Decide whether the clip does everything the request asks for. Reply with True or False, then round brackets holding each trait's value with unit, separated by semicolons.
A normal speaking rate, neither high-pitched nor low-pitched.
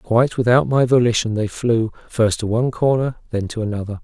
False (195 wpm; 115 Hz)